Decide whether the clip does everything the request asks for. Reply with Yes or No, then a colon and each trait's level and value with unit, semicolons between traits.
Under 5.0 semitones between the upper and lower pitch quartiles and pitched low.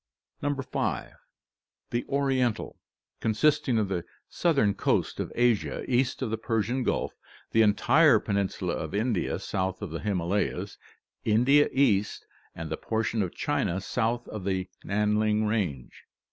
Yes: average, 3.9 semitones; low, 110 Hz